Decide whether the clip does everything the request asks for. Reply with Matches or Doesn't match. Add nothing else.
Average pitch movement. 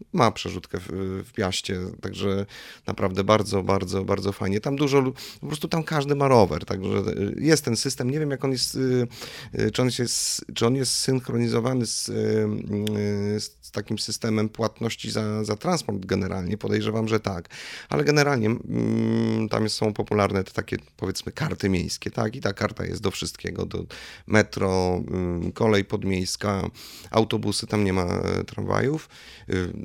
Matches